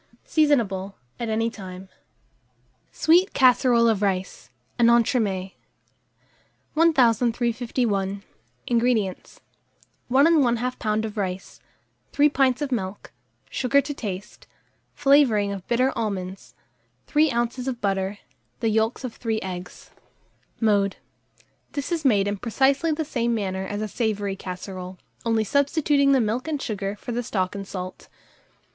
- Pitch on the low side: No, high, 225 Hz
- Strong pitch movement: No, average, 4.7 semitones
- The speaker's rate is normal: No, slow, 125 wpm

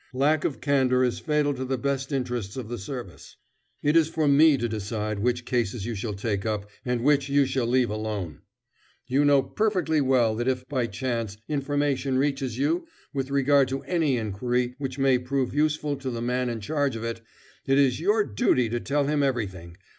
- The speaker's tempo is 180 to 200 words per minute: Yes, average, 195 wpm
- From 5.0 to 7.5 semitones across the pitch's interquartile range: No, average, 3.4 semitones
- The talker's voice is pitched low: Yes, low, 130 Hz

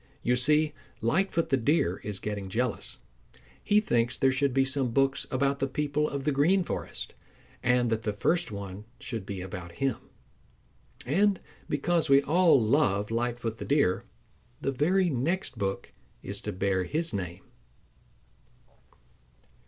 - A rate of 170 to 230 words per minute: No, average, 145 wpm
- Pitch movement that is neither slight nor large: No, wide, 5.8 semitones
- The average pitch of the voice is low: Yes, low, 130 Hz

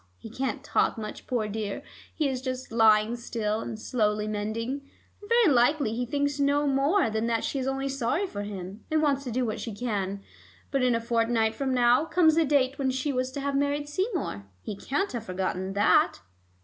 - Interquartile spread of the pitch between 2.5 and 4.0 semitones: No, average, 4.5 semitones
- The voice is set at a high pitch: Yes, very high, 250 Hz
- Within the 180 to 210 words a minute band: Yes, fast, 205 wpm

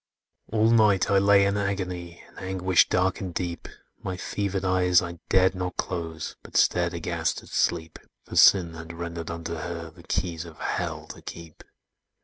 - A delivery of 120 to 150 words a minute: No, average, 170 wpm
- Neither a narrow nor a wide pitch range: No, narrow, 2.1 semitones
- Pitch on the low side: Yes, very low, 90 Hz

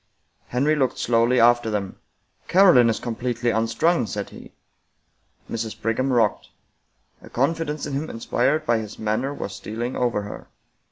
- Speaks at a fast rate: No, average, 150 wpm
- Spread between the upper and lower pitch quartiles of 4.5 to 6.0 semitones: No, average, 3.4 semitones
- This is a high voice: No, low, 120 Hz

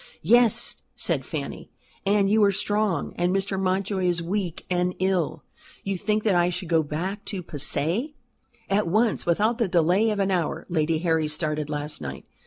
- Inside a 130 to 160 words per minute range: No, average, 175 wpm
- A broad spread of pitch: No, average, 3.7 semitones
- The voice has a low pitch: No, medium, 185 Hz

